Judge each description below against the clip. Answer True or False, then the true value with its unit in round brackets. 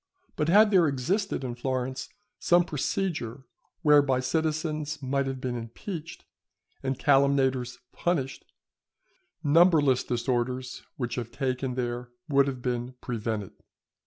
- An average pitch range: True (3.4 semitones)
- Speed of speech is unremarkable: False (115 wpm)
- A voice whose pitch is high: False (135 Hz)